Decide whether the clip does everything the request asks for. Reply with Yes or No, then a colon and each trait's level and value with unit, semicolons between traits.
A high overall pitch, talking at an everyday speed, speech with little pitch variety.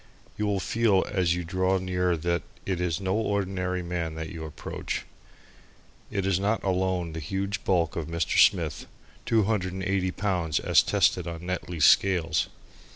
No: very low, 90 Hz; average, 165 wpm; narrow, 2.3 semitones